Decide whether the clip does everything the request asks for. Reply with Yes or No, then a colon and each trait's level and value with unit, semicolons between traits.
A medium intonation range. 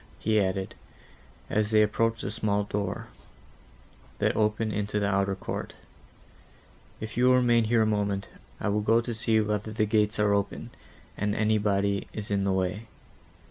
No: narrow, 1.4 semitones